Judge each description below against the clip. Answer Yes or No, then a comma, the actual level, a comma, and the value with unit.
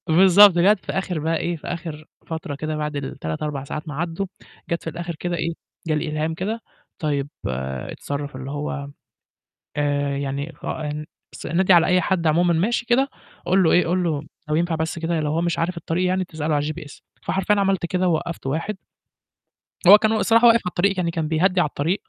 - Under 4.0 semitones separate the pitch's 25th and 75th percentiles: Yes, average, 3.2 semitones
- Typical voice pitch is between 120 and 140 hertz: No, medium, 165 Hz